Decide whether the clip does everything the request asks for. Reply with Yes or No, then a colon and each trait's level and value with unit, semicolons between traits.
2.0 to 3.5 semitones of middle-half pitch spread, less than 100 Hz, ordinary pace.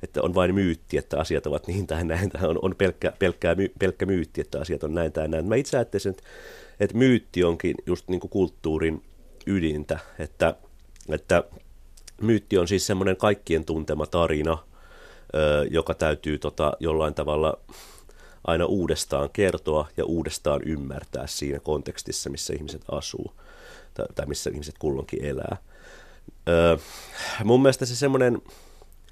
No: average, 4.2 semitones; very low, 85 Hz; average, 135 wpm